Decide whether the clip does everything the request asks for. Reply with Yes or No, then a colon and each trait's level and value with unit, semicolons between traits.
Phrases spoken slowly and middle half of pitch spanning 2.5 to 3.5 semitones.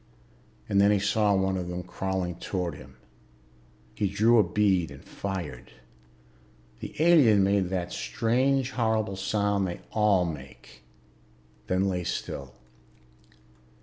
Yes: slow, 125 wpm; average, 2.9 semitones